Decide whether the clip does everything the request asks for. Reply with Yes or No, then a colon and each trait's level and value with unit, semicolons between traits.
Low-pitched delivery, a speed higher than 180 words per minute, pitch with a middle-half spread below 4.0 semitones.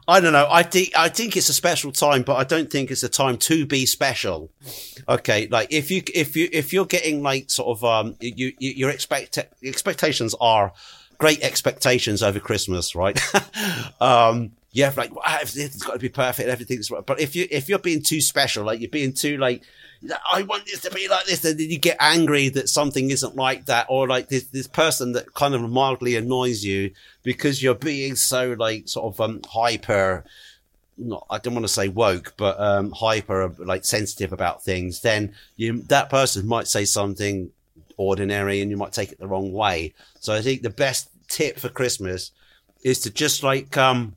No: low, 125 Hz; average, 200 wpm; average, 4.8 semitones